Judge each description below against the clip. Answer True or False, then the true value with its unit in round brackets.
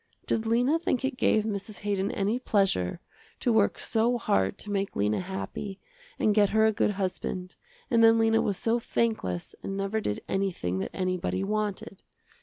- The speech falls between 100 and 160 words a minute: False (175 wpm)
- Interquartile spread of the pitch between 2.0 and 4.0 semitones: True (2.8 semitones)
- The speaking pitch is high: True (205 Hz)